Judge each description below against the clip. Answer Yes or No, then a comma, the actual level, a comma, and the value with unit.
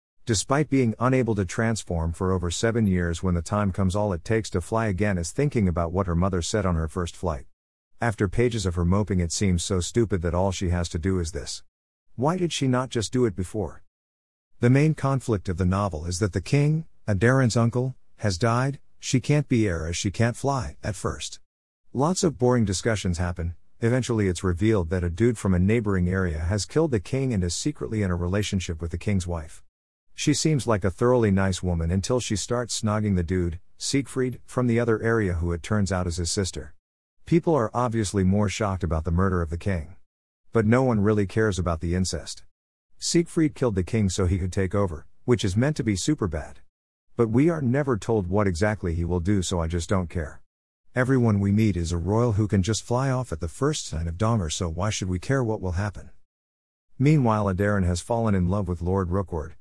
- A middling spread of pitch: Yes, average, 4.9 semitones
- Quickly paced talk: Yes, fast, 220 wpm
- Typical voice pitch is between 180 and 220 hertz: No, low, 100 Hz